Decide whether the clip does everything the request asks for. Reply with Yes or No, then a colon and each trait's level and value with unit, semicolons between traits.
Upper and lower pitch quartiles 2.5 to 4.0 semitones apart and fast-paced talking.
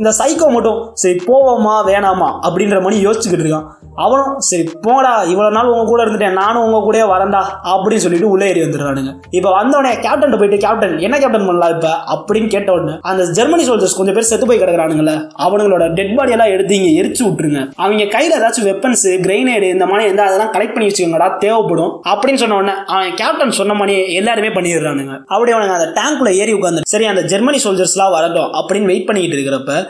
Yes: average, 3.7 semitones; fast, 180 wpm